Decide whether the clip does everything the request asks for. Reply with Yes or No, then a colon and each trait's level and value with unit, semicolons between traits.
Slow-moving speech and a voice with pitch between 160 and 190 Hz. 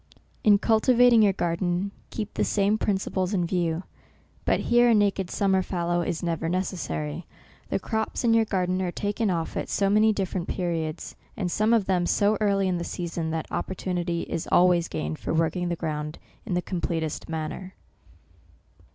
No: average, 175 wpm; medium, 185 Hz